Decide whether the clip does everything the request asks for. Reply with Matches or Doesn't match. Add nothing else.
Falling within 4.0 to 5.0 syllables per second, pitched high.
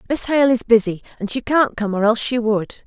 Doesn't match